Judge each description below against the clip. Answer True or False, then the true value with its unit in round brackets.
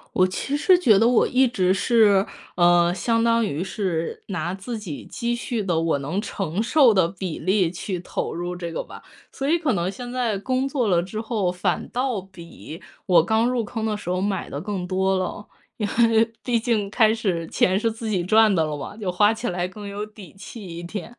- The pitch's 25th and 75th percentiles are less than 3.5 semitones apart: False (4.2 semitones)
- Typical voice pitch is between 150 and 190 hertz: False (200 Hz)